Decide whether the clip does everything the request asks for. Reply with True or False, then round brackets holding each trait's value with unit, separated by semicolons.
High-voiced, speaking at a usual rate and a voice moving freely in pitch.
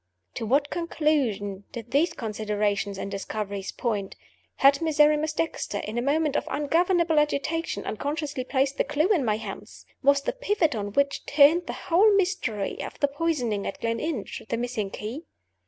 True (280 Hz; 160 wpm; 6.5 semitones)